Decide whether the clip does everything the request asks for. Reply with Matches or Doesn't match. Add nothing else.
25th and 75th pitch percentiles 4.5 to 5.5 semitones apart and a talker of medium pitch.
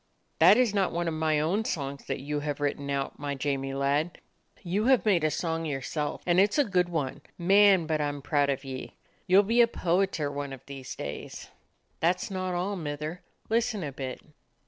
Matches